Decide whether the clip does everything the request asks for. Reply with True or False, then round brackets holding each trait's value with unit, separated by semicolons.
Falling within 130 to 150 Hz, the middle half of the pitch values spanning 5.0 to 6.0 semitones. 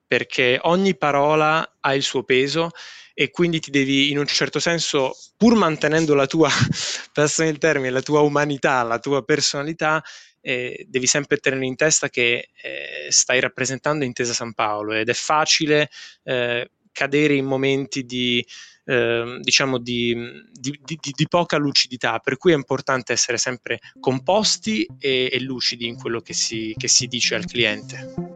False (140 Hz; 3.6 semitones)